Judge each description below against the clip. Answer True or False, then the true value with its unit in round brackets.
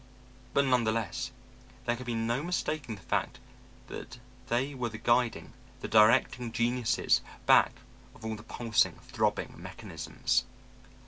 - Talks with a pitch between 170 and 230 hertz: False (120 Hz)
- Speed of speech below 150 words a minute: True (140 wpm)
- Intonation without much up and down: True (2.1 semitones)